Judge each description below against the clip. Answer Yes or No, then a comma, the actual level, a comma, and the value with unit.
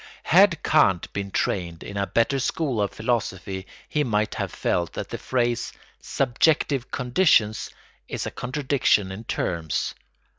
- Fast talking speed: No, average, 140 wpm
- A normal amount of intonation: No, wide, 5.7 semitones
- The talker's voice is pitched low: Yes, low, 115 Hz